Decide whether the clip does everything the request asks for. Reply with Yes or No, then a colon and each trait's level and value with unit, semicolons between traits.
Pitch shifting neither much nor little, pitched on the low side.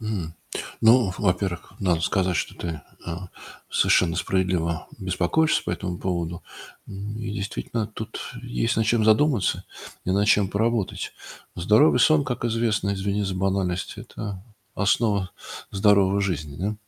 Yes: average, 3.3 semitones; low, 100 Hz